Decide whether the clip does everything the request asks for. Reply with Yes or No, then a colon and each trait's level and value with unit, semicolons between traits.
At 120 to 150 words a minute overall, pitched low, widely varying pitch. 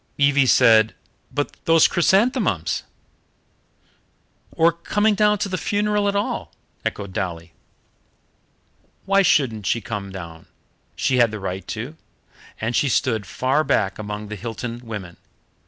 Yes: average, 140 wpm; low, 120 Hz; wide, 8.6 semitones